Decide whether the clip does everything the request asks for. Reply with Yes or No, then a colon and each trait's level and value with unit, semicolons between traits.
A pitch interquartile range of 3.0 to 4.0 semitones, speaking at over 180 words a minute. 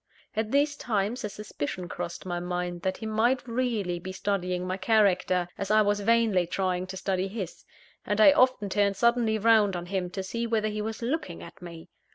Yes: average, 3.5 semitones; average, 200 wpm